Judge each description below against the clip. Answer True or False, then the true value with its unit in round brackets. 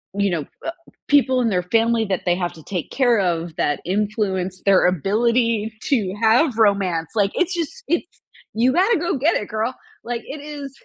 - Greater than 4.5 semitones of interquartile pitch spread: True (5.6 semitones)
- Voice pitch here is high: True (220 Hz)